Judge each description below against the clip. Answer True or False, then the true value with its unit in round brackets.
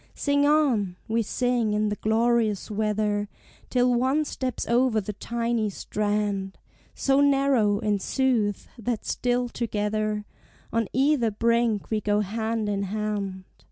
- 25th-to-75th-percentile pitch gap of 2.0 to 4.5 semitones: True (2.9 semitones)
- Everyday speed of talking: False (130 wpm)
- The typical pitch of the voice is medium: False (220 Hz)